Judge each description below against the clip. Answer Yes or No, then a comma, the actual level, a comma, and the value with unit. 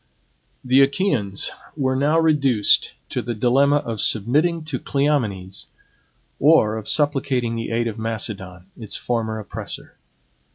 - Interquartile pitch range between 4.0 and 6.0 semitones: Yes, average, 4.4 semitones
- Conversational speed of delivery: No, slow, 125 wpm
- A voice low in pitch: Yes, low, 120 Hz